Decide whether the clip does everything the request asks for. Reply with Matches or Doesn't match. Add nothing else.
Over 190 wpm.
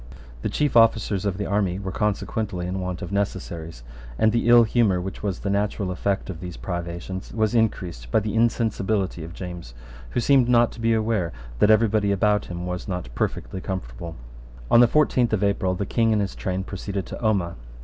Matches